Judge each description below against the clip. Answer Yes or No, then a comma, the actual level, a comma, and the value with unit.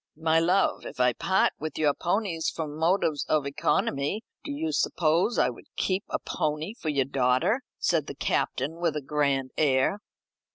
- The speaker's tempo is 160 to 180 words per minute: Yes, average, 170 wpm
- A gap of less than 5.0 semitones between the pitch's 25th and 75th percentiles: Yes, average, 4.4 semitones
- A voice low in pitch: No, medium, 155 Hz